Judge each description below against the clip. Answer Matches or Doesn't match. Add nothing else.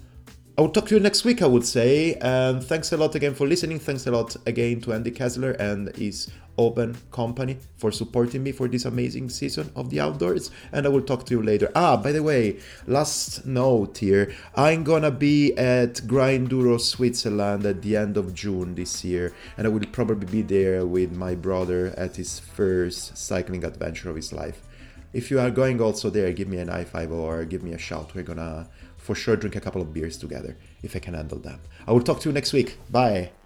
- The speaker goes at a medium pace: Doesn't match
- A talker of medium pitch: Doesn't match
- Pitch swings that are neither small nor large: Doesn't match